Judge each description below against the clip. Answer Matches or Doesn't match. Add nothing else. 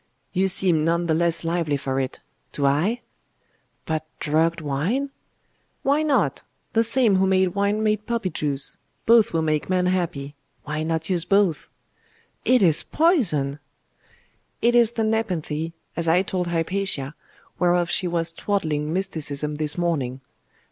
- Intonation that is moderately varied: Matches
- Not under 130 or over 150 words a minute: Matches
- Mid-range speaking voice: Matches